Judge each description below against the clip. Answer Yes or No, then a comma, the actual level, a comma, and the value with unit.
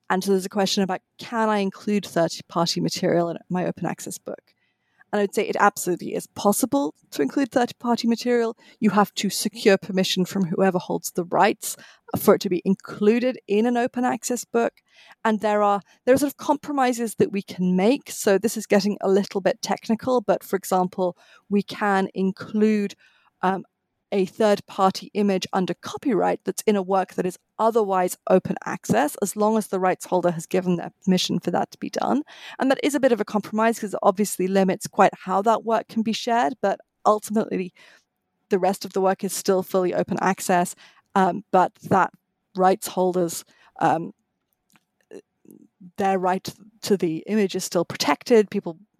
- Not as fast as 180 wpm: No, average, 185 wpm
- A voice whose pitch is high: Yes, high, 200 Hz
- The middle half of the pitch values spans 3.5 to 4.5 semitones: No, average, 2.9 semitones